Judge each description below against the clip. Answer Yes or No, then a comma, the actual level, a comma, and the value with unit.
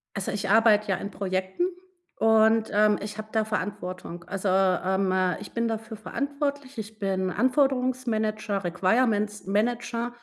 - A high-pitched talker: Yes, high, 215 Hz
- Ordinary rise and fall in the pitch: Yes, average, 3.1 semitones